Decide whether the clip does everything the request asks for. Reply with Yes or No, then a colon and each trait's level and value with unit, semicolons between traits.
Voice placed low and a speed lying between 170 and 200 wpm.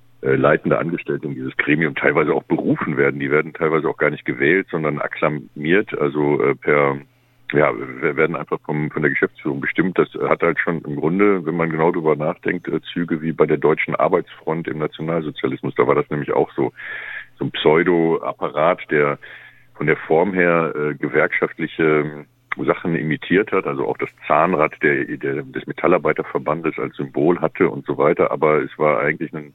Yes: very low, 75 Hz; average, 180 wpm